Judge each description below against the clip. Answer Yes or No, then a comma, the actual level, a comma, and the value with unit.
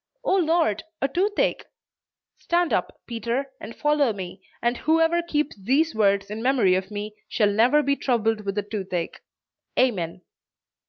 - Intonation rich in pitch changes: Yes, wide, 6.6 semitones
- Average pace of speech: Yes, average, 150 wpm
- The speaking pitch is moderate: No, high, 235 Hz